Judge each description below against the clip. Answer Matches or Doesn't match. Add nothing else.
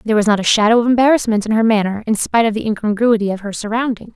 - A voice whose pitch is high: Matches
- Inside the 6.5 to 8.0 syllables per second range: Matches